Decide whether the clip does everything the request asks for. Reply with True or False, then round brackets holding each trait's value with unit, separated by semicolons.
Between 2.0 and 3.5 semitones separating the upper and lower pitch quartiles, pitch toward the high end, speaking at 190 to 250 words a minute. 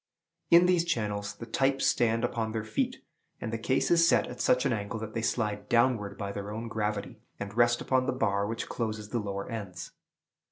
False (2.9 semitones; 115 Hz; 205 wpm)